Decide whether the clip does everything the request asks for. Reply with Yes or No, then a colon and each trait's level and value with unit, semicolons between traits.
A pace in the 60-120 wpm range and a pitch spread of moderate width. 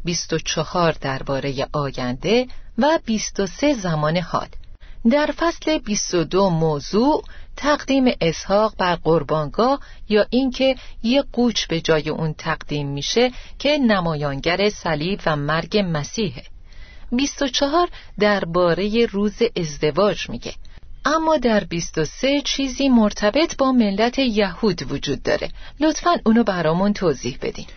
No: average, 110 wpm; wide, 8.2 semitones